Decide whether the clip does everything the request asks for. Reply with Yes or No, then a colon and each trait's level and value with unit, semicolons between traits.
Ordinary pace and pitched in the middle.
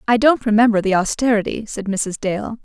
No: average, 180 wpm; high, 215 Hz